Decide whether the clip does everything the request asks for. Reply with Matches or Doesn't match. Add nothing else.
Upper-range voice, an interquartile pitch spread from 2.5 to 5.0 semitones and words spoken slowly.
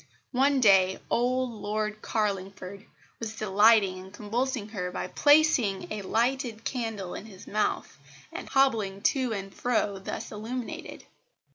Matches